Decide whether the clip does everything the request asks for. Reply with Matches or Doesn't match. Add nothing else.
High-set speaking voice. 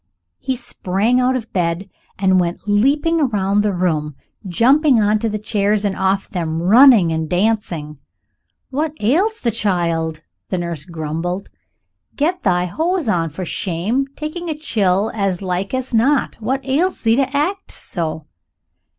Matches